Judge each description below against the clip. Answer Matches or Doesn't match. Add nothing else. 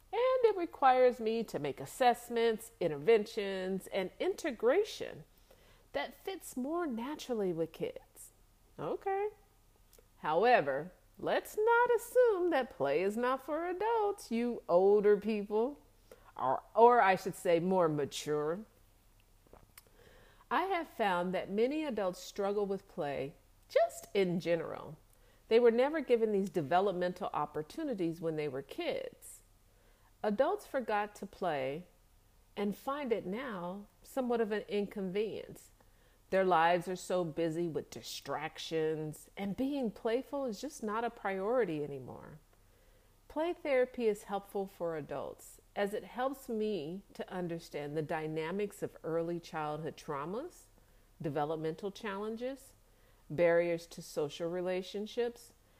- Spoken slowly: Matches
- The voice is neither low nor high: Doesn't match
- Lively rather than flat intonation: Matches